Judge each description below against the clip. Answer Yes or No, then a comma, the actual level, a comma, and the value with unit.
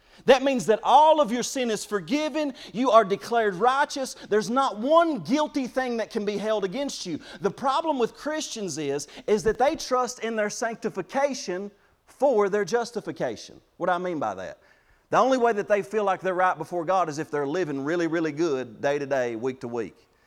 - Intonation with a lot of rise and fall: Yes, wide, 6.5 semitones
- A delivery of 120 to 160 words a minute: No, fast, 205 wpm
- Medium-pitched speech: No, high, 215 Hz